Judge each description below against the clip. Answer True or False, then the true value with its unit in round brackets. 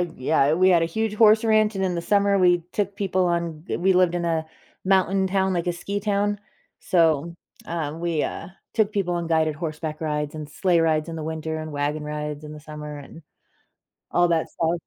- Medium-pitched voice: True (170 Hz)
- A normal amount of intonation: True (3.5 semitones)